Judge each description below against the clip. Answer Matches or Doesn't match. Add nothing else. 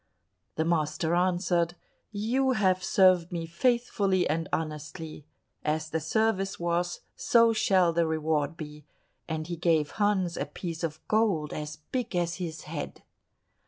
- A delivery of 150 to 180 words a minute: Doesn't match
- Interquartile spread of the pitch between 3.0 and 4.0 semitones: Matches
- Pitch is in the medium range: Matches